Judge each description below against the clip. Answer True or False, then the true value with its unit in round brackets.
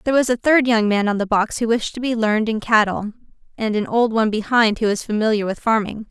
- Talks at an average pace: False (255 wpm)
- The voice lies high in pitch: True (220 Hz)